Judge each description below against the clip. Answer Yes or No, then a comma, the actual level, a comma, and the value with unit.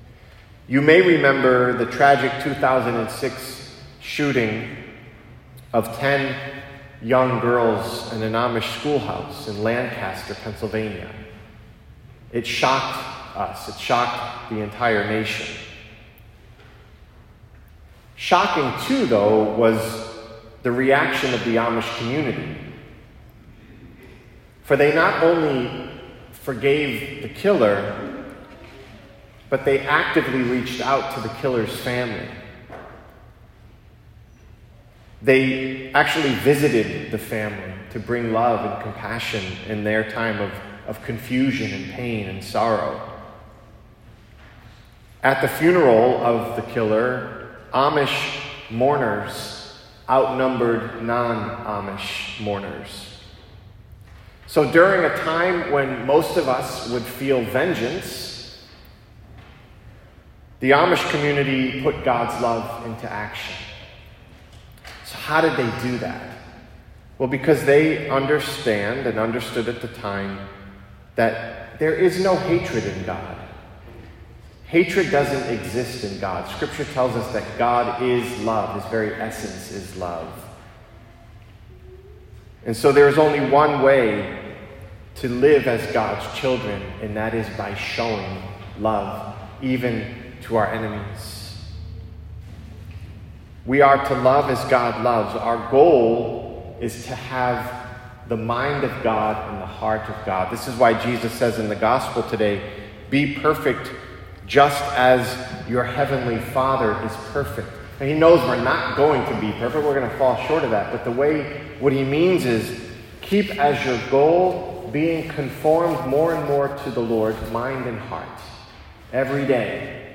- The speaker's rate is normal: No, slow, 120 wpm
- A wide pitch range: No, average, 3.8 semitones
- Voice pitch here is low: Yes, low, 115 Hz